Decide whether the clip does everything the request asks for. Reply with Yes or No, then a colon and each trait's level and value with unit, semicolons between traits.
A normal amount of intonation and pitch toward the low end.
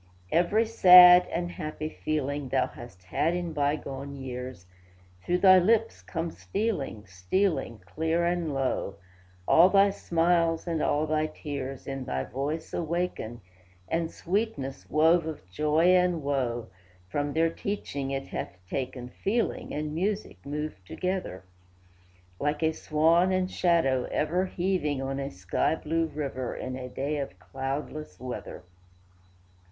No: average, 4.5 semitones; medium, 155 Hz